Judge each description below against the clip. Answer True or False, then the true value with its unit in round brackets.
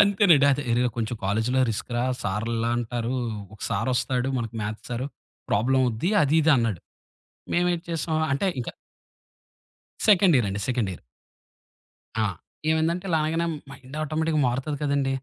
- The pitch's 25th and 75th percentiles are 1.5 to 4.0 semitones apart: False (5.3 semitones)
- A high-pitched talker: False (130 Hz)